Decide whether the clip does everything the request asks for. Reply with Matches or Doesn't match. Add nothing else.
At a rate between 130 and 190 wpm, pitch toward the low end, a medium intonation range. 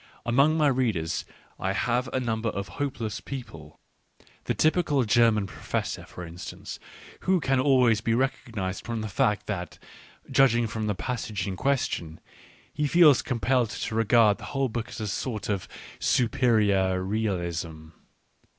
Matches